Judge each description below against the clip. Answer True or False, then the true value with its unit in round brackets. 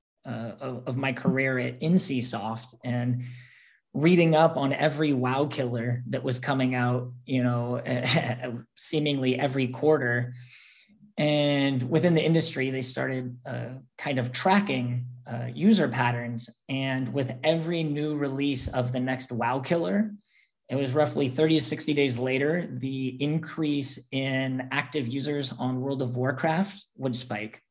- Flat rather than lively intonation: False (3.3 semitones)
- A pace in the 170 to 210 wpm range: False (140 wpm)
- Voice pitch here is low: True (130 Hz)